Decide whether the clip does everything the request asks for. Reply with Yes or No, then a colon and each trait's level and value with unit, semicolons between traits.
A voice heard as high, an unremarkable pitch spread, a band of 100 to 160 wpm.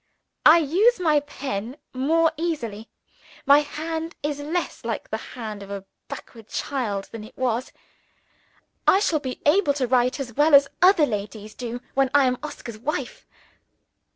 Yes: very high, 275 Hz; average, 4.9 semitones; average, 155 wpm